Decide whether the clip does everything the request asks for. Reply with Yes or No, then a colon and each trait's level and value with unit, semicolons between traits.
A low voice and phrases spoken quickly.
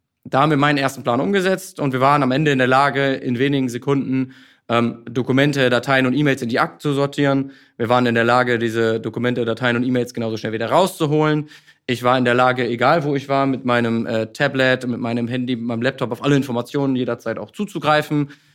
Yes: low, 130 Hz; fast, 215 wpm